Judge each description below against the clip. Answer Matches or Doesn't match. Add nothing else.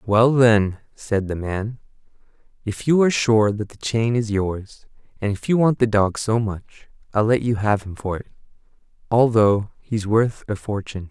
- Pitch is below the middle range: Matches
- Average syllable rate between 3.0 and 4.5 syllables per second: Matches